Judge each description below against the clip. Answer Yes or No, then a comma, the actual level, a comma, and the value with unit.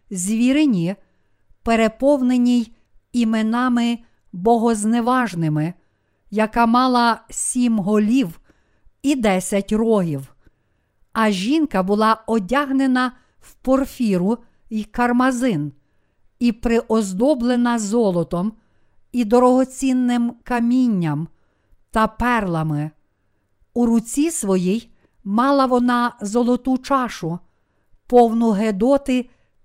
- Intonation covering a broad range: No, average, 4.4 semitones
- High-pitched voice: Yes, high, 230 Hz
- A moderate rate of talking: No, slow, 75 wpm